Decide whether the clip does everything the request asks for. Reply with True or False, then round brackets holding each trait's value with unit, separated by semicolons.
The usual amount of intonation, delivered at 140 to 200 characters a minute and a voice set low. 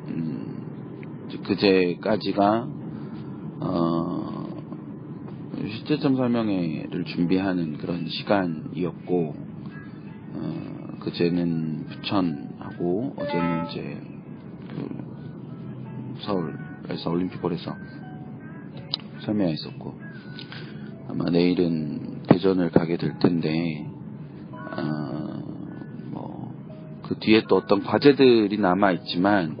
True (3.4 semitones; 170 characters per minute; 90 Hz)